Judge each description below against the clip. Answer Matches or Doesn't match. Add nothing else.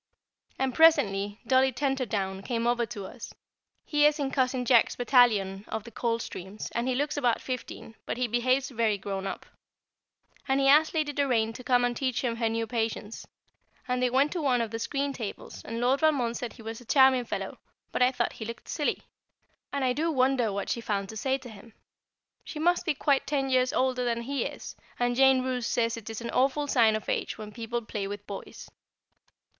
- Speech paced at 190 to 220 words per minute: Matches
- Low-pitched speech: Doesn't match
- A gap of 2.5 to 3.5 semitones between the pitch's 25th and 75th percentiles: Matches